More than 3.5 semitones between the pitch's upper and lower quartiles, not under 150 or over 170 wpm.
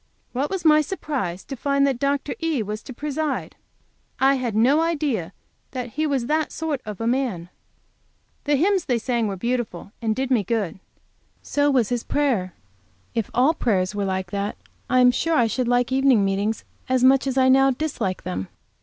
No: average, 4.7 semitones; average, 190 wpm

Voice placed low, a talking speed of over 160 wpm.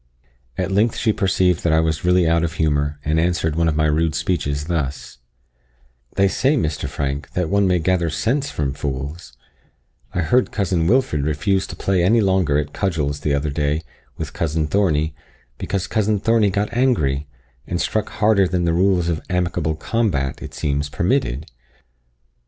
Yes: very low, 85 Hz; average, 170 wpm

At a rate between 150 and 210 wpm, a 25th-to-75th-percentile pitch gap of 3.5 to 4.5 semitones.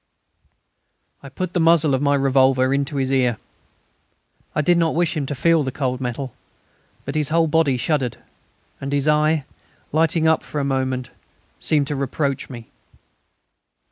No: average, 160 wpm; average, 3.0 semitones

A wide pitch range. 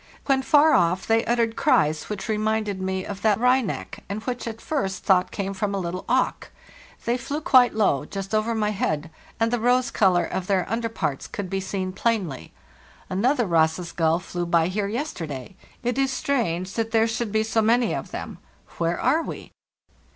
No: average, 4.2 semitones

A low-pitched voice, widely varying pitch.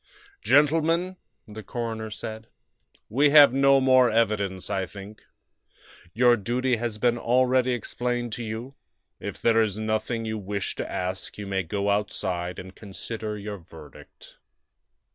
No: low, 110 Hz; average, 3.5 semitones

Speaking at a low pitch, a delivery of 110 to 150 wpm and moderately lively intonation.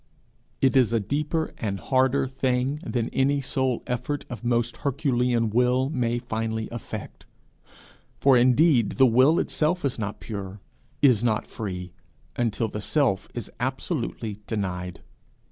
Yes: low, 125 Hz; slow, 135 wpm; average, 3.2 semitones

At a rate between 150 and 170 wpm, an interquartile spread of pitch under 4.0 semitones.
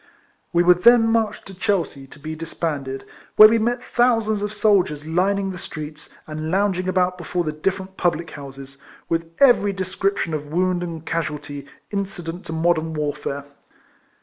No: average, 160 wpm; average, 4.4 semitones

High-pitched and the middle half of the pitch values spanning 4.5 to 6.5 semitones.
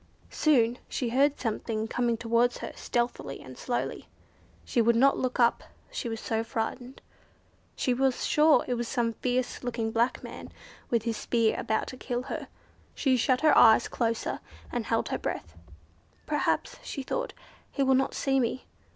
No: high, 245 Hz; narrow, 2.4 semitones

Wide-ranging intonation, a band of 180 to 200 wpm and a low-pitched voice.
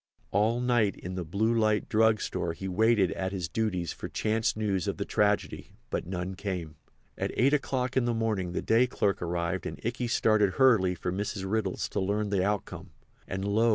No: average, 3.3 semitones; average, 195 wpm; low, 105 Hz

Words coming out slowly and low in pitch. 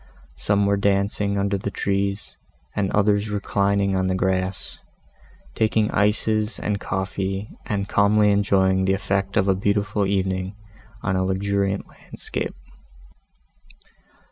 Yes: slow, 120 wpm; low, 100 Hz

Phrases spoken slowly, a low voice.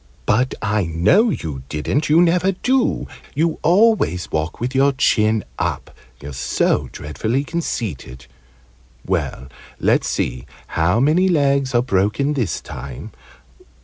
Yes: slow, 125 wpm; low, 125 Hz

